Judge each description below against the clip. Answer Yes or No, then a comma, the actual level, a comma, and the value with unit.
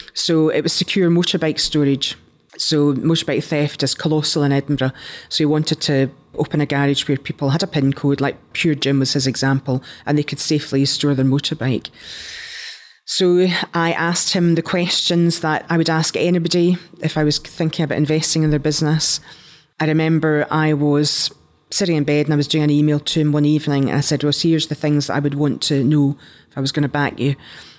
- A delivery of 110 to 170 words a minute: No, fast, 205 wpm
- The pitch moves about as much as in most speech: No, narrow, 2.3 semitones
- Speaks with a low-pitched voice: No, medium, 150 Hz